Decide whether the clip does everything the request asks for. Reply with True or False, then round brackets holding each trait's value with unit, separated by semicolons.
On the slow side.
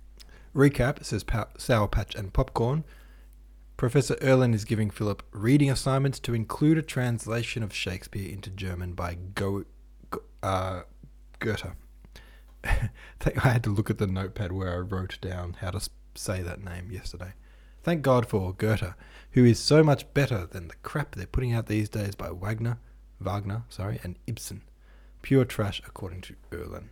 False (160 wpm)